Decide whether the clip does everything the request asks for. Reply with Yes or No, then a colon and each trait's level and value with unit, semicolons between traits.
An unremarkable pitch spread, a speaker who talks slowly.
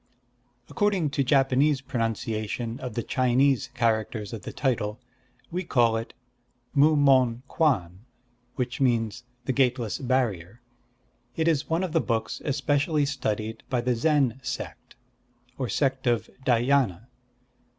Yes: average, 3.5 semitones; slow, 130 wpm